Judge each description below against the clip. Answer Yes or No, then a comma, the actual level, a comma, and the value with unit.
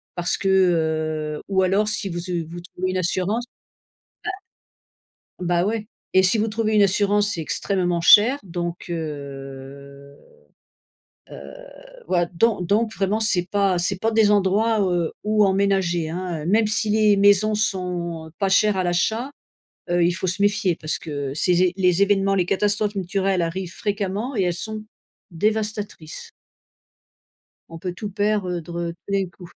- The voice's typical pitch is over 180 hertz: Yes, high, 190 Hz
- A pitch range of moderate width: Yes, average, 3.2 semitones